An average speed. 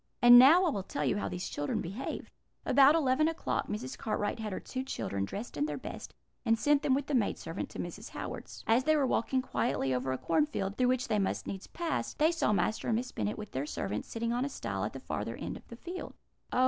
No: fast, 250 wpm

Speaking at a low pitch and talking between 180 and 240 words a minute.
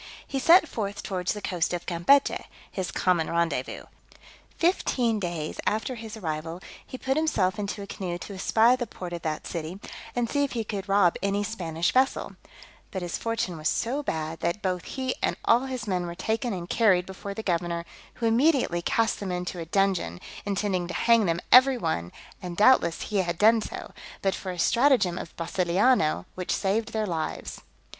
No: high, 195 Hz; average, 185 wpm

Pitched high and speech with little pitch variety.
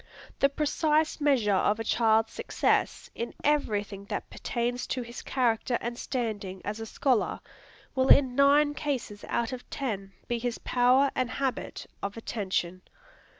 No: high, 240 Hz; average, 3.9 semitones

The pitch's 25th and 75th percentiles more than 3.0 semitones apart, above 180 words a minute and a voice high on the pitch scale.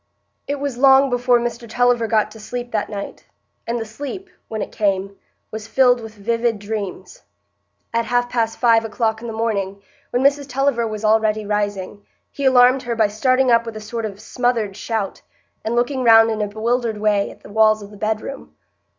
No: narrow, 2.5 semitones; average, 195 wpm; high, 225 Hz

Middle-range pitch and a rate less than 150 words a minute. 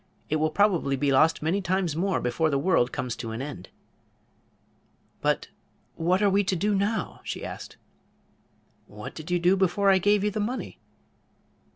No: medium, 180 Hz; average, 175 wpm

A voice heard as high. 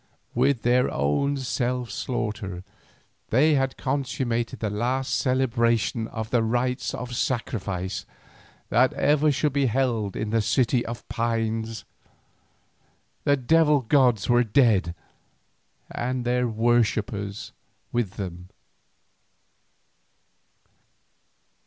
No: low, 120 Hz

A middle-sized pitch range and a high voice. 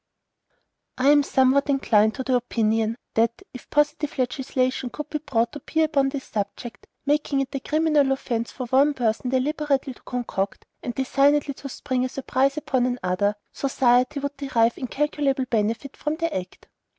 Yes: average, 3.0 semitones; very high, 265 Hz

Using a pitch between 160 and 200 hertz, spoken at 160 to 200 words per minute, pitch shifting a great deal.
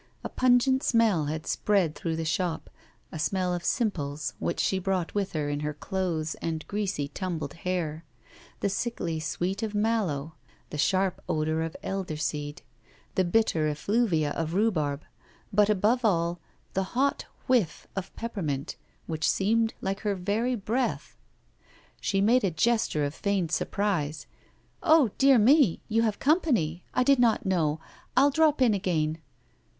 No: high, 190 Hz; average, 150 wpm; wide, 5.9 semitones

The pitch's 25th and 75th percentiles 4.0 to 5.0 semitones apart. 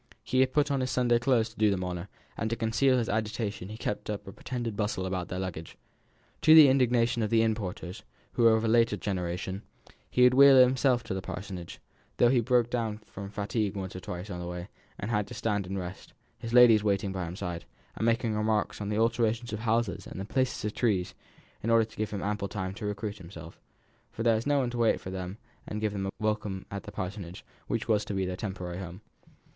No: average, 3.4 semitones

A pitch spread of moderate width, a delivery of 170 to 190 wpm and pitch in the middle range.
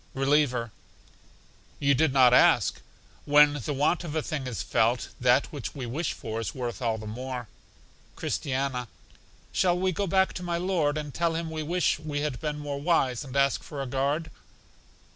Yes: average, 3.8 semitones; average, 180 wpm; medium, 145 Hz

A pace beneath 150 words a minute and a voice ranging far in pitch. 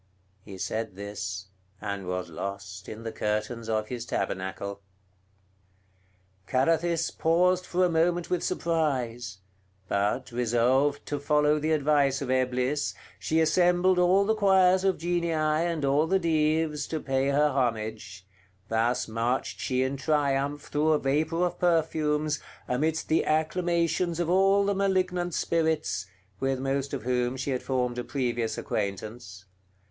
Yes: average, 140 wpm; wide, 5.8 semitones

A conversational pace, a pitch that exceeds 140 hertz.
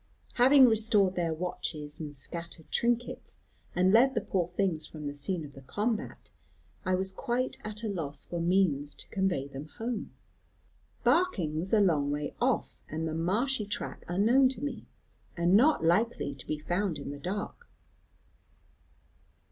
Yes: average, 160 wpm; medium, 185 Hz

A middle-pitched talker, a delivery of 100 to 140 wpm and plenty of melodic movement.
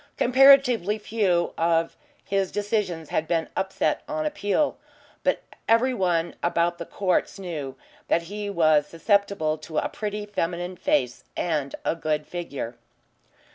No: medium, 175 Hz; slow, 135 wpm; average, 4.2 semitones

